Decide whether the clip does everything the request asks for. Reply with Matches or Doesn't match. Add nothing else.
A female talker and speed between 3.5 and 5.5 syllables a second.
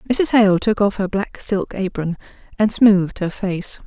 Matches